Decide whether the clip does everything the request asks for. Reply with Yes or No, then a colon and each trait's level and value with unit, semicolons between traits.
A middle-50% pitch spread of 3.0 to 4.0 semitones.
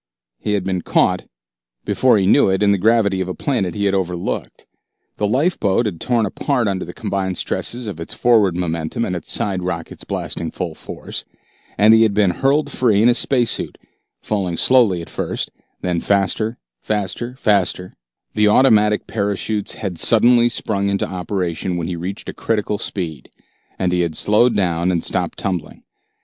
Yes: average, 3.7 semitones